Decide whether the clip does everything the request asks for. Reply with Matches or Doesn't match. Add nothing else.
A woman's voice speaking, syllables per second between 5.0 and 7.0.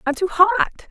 Matches